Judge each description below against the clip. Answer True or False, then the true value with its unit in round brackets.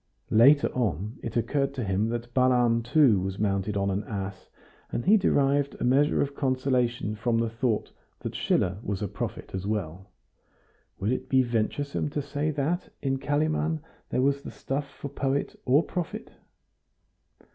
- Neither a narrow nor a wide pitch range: True (4.9 semitones)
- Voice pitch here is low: True (125 Hz)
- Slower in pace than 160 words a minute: False (165 wpm)